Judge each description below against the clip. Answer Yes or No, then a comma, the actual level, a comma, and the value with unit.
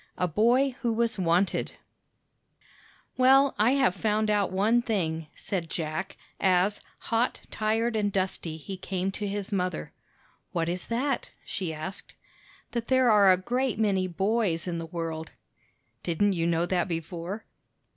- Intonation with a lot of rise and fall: No, average, 4.5 semitones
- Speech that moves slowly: No, average, 145 wpm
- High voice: Yes, high, 195 Hz